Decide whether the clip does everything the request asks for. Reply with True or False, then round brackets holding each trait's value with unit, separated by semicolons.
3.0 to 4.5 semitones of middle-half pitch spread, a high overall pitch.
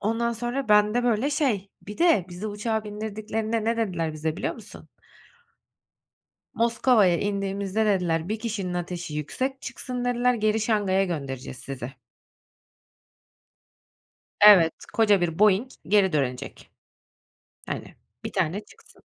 True (4.2 semitones; 210 Hz)